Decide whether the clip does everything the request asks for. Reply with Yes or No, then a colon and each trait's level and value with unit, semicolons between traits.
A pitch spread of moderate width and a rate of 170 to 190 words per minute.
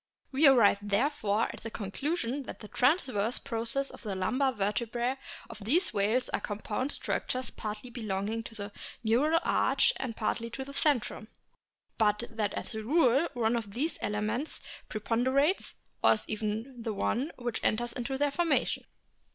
No: average, 4.0 semitones; average, 160 wpm